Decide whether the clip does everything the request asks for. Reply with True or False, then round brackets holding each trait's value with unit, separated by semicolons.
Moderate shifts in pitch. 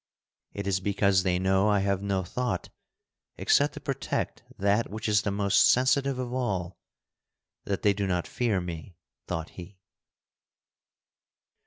False (2.2 semitones)